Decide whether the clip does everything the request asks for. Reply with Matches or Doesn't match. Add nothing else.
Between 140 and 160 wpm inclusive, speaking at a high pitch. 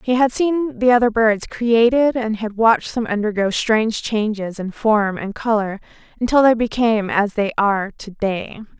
Doesn't match